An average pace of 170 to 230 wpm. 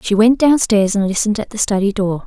No: fast, 265 wpm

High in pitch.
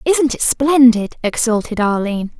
Yes: high, 240 Hz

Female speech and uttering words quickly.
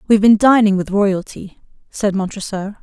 No: female; average, 170 wpm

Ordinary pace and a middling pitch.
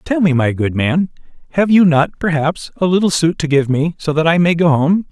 No: fast, 245 wpm; medium, 160 Hz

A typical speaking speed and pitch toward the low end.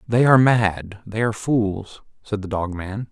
Yes: average, 190 wpm; low, 105 Hz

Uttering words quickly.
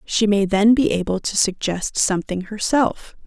No: average, 165 wpm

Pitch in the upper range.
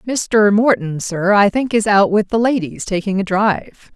Yes: high, 205 Hz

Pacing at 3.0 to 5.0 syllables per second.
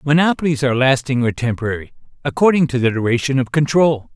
No: 6.5 syllables/s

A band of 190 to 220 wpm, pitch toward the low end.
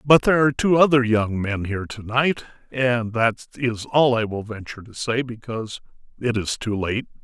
Yes: average, 200 wpm; low, 120 Hz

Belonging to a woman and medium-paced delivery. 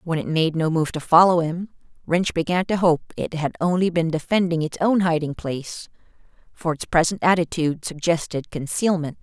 Yes: female; average, 175 wpm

